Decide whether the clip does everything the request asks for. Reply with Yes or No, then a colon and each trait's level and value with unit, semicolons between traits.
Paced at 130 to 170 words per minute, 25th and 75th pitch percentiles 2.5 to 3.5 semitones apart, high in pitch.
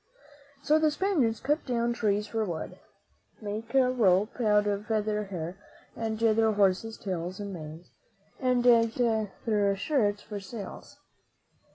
Yes: slow, 135 wpm; average, 2.9 semitones; high, 215 Hz